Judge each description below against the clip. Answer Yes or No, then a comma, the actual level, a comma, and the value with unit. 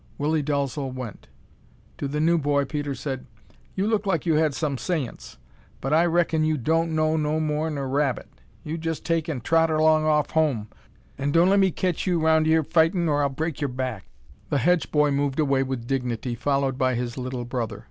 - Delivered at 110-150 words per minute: No, average, 200 wpm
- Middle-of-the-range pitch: Yes, medium, 150 Hz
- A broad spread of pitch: No, average, 3.1 semitones